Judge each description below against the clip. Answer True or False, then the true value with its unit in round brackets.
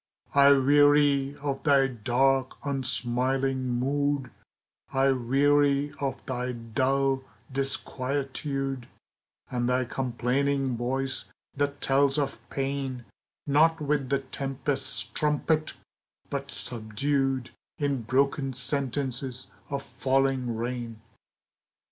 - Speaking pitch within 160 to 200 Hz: False (135 Hz)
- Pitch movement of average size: False (1.7 semitones)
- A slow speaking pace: True (95 wpm)